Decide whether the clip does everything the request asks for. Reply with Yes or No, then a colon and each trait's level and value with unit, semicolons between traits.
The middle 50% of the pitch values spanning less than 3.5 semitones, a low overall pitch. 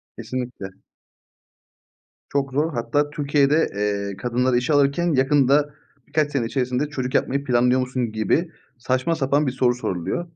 Yes: average, 2.9 semitones; low, 130 Hz